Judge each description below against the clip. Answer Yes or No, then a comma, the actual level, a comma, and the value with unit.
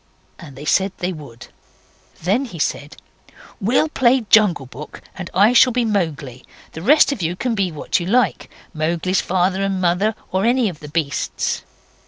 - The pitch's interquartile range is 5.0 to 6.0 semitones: Yes, wide, 5.6 semitones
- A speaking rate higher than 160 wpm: Yes, average, 175 wpm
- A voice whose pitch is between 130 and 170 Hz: No, medium, 185 Hz